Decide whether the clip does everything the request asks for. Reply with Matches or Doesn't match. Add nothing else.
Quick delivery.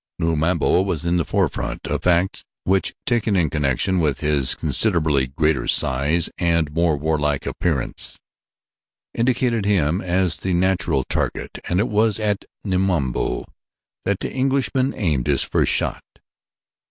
Doesn't match